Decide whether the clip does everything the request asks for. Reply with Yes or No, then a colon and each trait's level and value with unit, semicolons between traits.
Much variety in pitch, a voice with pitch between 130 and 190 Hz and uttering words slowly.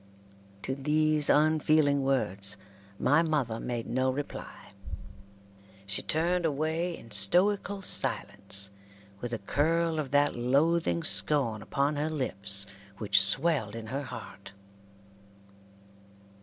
Yes: wide, 5.9 semitones; medium, 140 Hz; slow, 110 wpm